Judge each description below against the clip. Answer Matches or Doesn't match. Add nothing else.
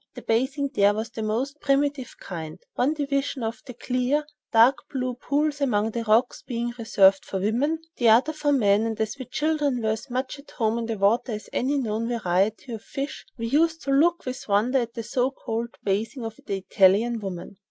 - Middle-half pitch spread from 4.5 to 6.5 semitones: Doesn't match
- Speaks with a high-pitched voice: Matches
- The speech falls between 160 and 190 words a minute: Doesn't match